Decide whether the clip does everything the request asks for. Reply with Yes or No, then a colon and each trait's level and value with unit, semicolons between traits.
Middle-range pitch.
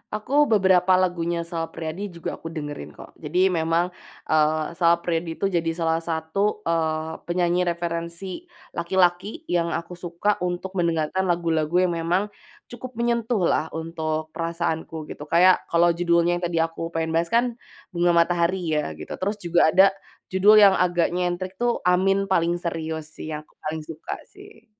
Yes: medium, 170 Hz